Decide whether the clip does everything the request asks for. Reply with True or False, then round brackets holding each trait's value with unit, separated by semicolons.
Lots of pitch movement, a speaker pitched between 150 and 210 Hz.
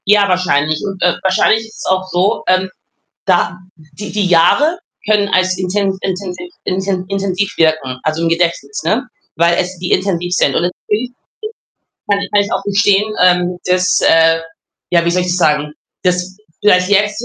False (2.4 semitones; 185 Hz)